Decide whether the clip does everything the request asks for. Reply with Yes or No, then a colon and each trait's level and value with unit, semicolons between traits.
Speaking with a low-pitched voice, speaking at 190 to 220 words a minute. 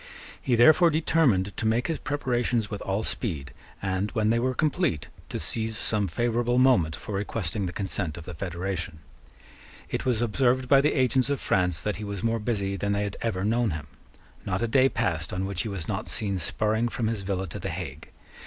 Yes: low, 110 Hz; fast, 205 wpm